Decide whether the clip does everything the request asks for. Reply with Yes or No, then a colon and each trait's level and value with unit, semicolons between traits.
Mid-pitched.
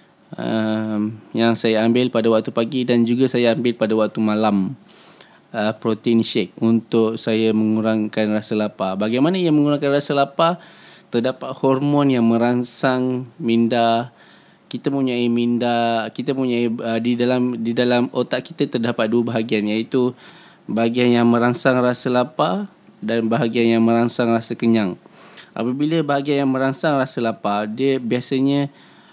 No: low, 120 Hz